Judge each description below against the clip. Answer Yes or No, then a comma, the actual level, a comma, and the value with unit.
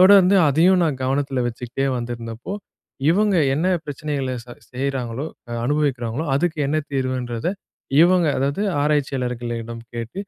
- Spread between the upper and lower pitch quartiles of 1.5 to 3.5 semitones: No, average, 4.4 semitones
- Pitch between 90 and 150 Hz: Yes, low, 135 Hz